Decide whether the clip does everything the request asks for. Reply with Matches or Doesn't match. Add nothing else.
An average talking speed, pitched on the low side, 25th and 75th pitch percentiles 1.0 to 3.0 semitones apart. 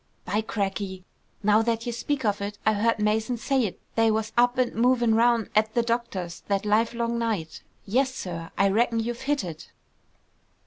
Doesn't match